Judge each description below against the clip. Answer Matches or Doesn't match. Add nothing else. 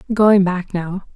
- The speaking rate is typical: Matches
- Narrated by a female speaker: Matches